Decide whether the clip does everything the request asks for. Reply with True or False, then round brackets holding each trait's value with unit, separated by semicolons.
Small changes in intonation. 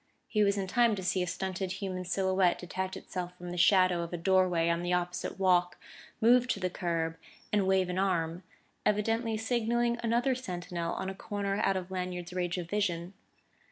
True (2.3 semitones)